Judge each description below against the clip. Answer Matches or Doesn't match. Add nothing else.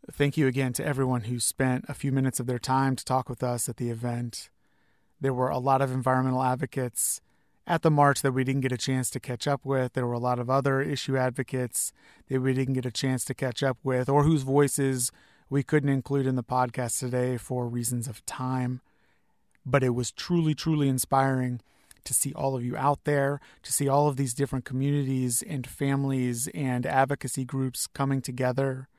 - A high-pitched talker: Doesn't match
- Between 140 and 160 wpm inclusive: Doesn't match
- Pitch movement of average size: Doesn't match